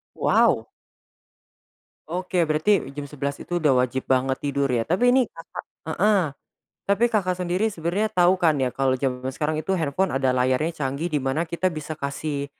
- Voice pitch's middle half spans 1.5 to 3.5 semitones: No, average, 4.8 semitones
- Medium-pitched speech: Yes, medium, 155 Hz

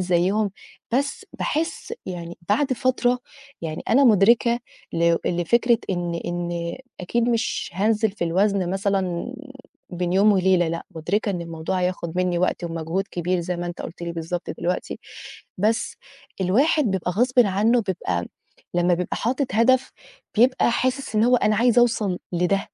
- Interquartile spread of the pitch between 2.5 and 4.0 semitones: No, average, 5.0 semitones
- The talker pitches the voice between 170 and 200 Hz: Yes, high, 190 Hz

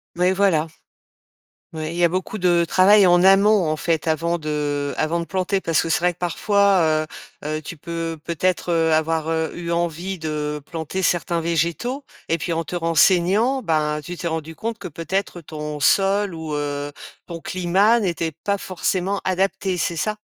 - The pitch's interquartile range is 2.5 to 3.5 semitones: Yes, average, 2.9 semitones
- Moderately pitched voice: Yes, medium, 170 Hz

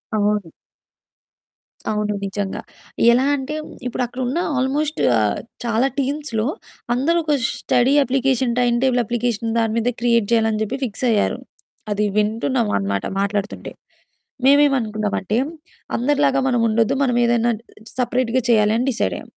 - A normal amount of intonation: Yes, average, 3.5 semitones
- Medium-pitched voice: No, high, 235 Hz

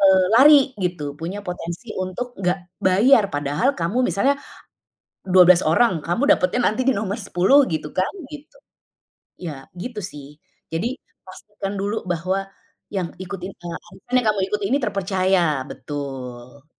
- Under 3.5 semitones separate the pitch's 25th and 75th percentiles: No, average, 3.9 semitones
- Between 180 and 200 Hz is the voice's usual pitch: Yes, high, 190 Hz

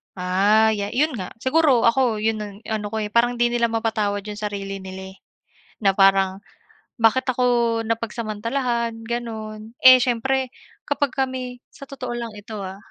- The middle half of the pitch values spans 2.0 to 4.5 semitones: Yes, average, 3.1 semitones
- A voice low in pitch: No, high, 225 Hz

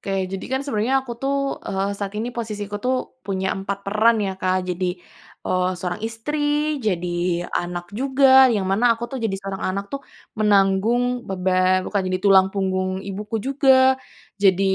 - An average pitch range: Yes, average, 3.3 semitones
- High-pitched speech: Yes, high, 200 Hz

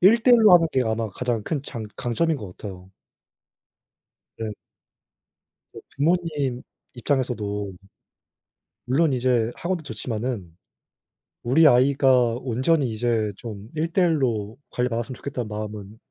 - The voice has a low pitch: Yes, low, 125 Hz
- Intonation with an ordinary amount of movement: Yes, average, 4.7 semitones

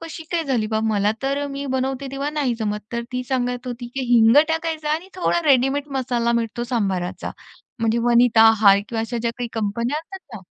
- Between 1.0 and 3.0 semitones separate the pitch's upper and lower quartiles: No, average, 3.7 semitones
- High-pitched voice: Yes, high, 245 Hz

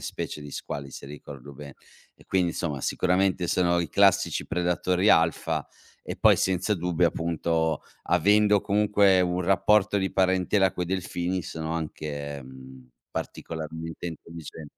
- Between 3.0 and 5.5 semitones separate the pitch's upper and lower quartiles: Yes, average, 3.4 semitones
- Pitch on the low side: Yes, very low, 85 Hz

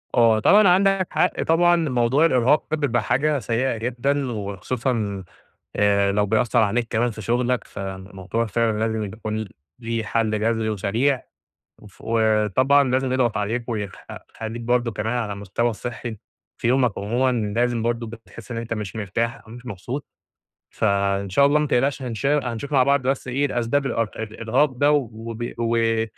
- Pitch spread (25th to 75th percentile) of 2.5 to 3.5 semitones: Yes, average, 3.0 semitones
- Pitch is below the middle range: Yes, low, 115 Hz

